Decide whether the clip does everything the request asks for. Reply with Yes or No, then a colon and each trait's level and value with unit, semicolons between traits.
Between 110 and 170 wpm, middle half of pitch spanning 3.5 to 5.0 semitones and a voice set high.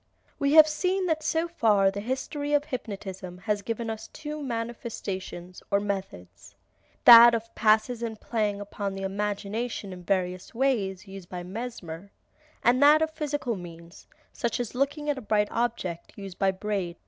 Yes: average, 160 wpm; average, 4.7 semitones; high, 215 Hz